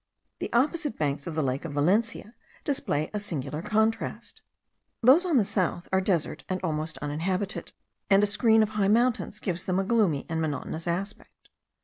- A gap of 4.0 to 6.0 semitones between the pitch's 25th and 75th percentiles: Yes, wide, 5.4 semitones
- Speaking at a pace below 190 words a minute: Yes, average, 170 wpm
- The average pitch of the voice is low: No, high, 190 Hz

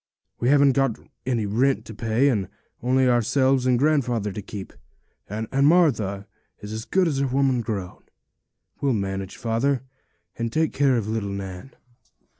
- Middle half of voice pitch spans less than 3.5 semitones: No, average, 4.5 semitones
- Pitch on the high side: No, low, 120 Hz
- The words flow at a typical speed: Yes, average, 155 wpm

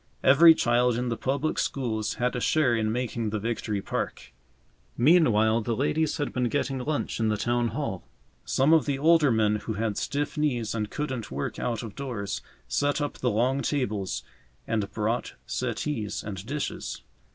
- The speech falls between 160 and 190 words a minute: Yes, average, 175 wpm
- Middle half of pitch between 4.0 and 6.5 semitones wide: Yes, average, 4.5 semitones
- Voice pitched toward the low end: Yes, low, 120 Hz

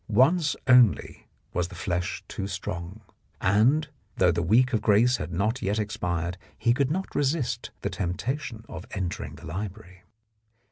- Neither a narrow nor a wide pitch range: No, wide, 5.8 semitones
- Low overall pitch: Yes, low, 105 Hz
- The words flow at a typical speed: Yes, average, 150 wpm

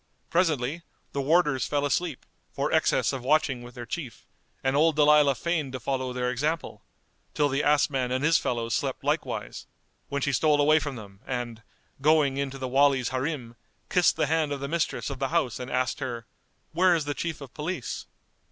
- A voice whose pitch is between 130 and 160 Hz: Yes, medium, 140 Hz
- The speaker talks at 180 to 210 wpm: Yes, average, 195 wpm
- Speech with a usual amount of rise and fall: Yes, average, 3.1 semitones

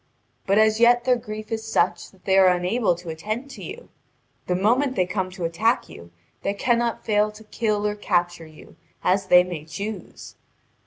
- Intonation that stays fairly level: No, average, 3.8 semitones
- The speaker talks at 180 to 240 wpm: Yes, average, 190 wpm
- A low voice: No, high, 205 Hz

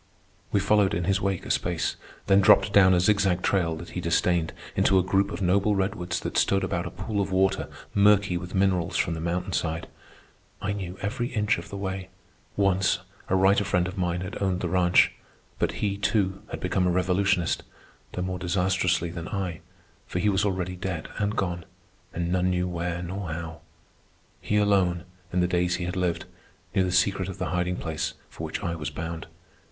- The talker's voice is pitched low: Yes, very low, 95 Hz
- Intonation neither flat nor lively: No, narrow, 1.9 semitones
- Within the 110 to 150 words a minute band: No, average, 200 wpm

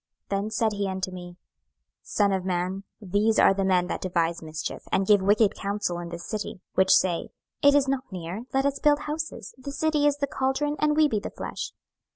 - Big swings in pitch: Yes, wide, 6.6 semitones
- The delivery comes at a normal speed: No, fast, 215 wpm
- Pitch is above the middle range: Yes, high, 205 Hz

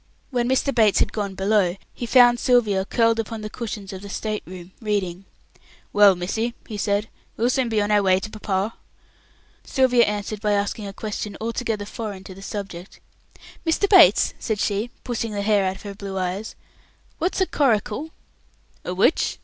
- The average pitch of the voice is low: No, high, 210 Hz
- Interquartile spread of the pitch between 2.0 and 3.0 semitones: Yes, average, 2.7 semitones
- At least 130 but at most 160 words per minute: No, average, 180 wpm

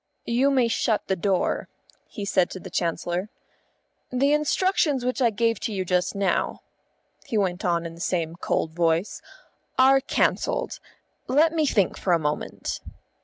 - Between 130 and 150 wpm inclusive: No, average, 160 wpm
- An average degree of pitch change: No, wide, 6.7 semitones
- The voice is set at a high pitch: Yes, high, 200 Hz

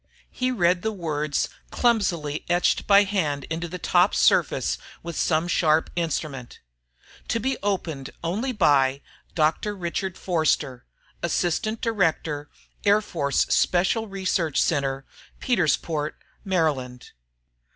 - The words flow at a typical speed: No, slow, 110 wpm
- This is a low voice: No, medium, 170 Hz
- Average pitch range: Yes, average, 4.7 semitones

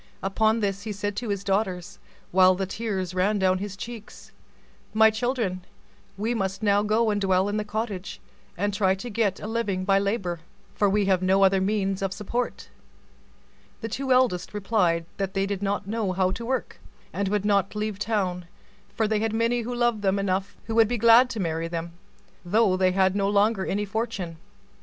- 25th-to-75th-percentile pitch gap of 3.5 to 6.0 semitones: No, narrow, 2.6 semitones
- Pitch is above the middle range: Yes, high, 200 Hz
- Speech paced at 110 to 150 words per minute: No, average, 185 wpm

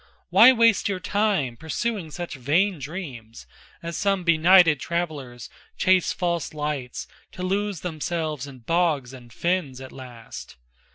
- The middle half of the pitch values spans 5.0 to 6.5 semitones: Yes, wide, 5.6 semitones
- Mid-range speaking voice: Yes, medium, 160 Hz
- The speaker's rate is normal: No, slow, 130 wpm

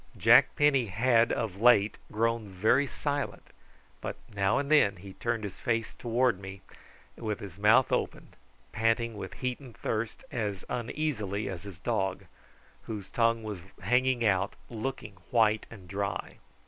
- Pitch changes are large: No, average, 3.3 semitones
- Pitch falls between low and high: No, low, 110 Hz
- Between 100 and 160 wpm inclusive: Yes, average, 150 wpm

